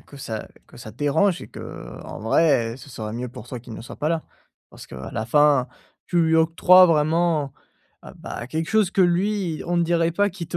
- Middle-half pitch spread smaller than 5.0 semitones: No, wide, 5.6 semitones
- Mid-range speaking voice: Yes, medium, 160 Hz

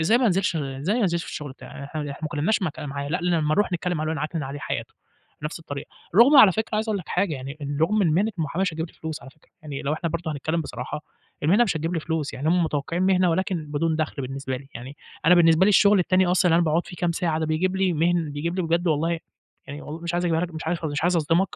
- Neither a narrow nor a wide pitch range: Yes, average, 3.1 semitones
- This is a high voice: No, medium, 165 Hz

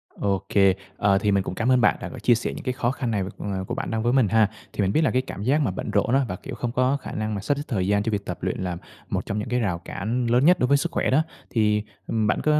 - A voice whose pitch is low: Yes, low, 110 Hz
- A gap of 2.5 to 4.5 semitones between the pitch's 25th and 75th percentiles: Yes, average, 3.9 semitones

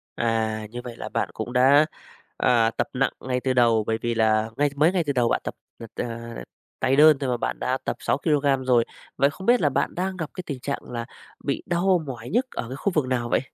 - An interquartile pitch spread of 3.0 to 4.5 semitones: Yes, average, 4.0 semitones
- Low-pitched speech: Yes, low, 130 Hz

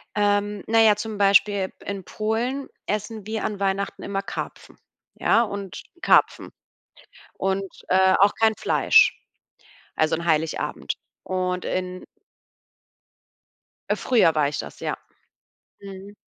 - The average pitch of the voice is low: No, high, 200 Hz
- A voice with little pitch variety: Yes, narrow, 2.2 semitones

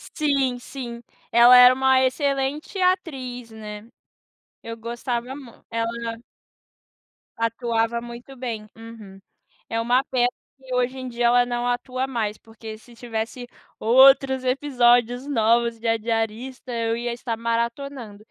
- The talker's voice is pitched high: Yes, high, 240 Hz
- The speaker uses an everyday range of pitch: No, narrow, 2.2 semitones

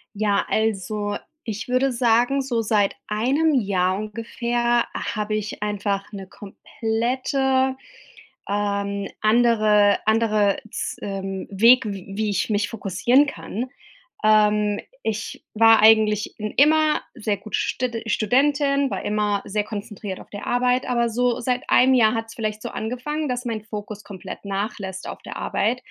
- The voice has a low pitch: No, high, 215 Hz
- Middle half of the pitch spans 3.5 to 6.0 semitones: No, average, 2.9 semitones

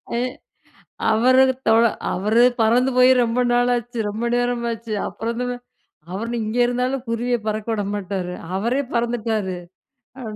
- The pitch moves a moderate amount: No, narrow, 2.1 semitones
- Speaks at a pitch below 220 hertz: No, high, 235 Hz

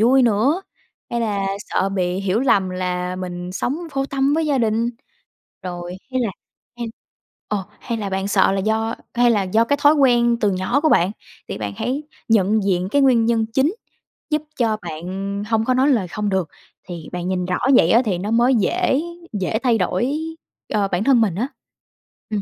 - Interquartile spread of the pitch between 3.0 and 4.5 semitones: No, average, 5.0 semitones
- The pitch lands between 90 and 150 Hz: No, high, 220 Hz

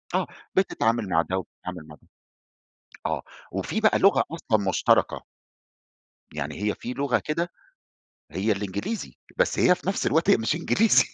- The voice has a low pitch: Yes, low, 110 Hz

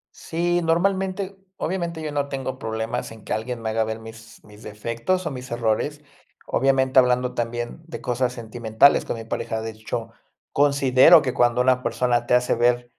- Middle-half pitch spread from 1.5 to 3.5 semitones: No, average, 4.1 semitones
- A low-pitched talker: Yes, low, 125 Hz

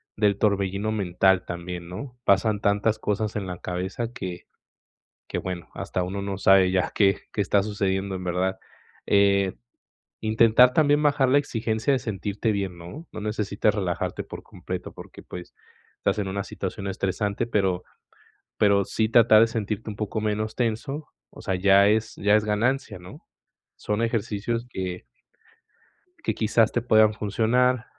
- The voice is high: No, low, 105 Hz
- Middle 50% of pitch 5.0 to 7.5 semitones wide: No, average, 2.7 semitones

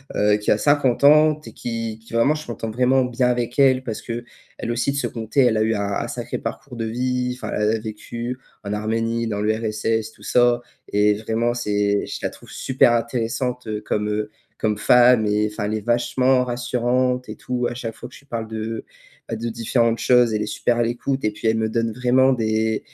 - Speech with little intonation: Yes, narrow, 2.3 semitones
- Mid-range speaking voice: No, low, 115 Hz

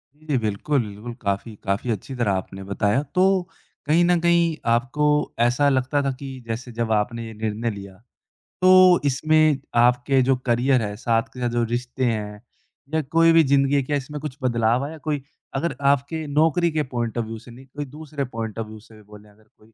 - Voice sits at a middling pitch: No, low, 125 Hz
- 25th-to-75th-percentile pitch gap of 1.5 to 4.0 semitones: No, average, 4.7 semitones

